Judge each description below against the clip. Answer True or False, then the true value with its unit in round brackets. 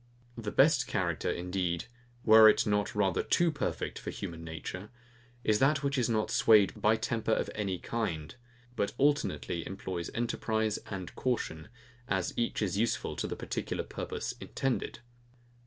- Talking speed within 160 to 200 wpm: False (150 wpm)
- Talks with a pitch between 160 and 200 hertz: False (105 Hz)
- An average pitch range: True (4.1 semitones)